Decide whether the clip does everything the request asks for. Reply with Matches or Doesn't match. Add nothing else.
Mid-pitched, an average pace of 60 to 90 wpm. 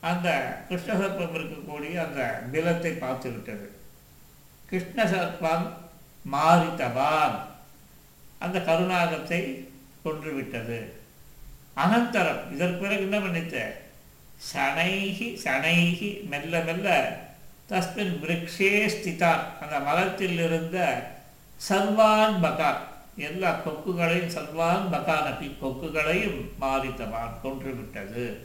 Matches